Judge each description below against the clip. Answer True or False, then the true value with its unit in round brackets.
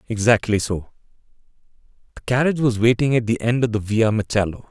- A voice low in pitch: True (115 Hz)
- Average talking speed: True (165 wpm)